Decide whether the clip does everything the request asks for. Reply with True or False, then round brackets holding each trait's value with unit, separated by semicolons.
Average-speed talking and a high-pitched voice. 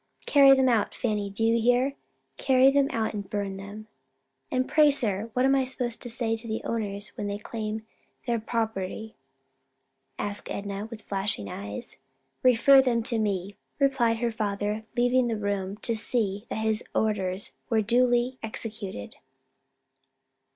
True (150 wpm; 220 Hz)